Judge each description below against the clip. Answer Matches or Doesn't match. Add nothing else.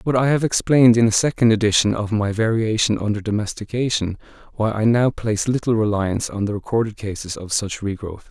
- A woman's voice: Doesn't match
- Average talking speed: Matches